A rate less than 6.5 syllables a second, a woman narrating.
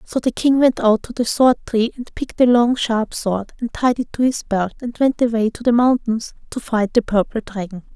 Yes: 5.1 syllables/s; female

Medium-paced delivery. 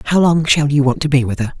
No: fast, 340 wpm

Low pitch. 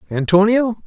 No: high, 205 Hz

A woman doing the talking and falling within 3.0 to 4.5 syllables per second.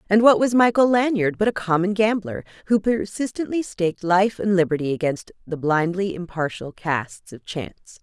No: female; 5.1 syllables/s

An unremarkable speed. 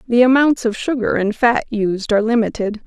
Yes: average, 190 wpm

